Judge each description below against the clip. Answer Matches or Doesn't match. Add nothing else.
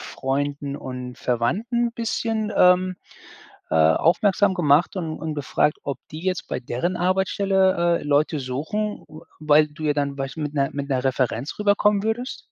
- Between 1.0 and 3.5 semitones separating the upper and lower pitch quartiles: Doesn't match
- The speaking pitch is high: Doesn't match